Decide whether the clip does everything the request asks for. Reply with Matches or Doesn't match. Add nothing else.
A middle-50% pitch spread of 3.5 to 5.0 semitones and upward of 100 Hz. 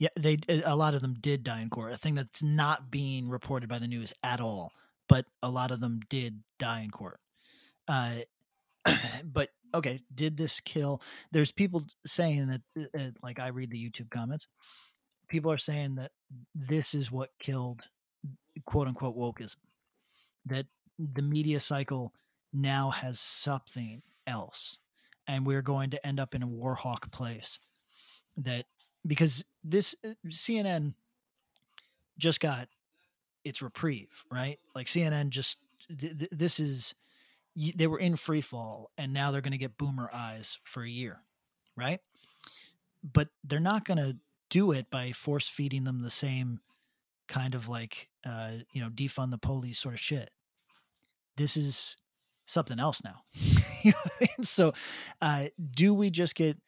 Matches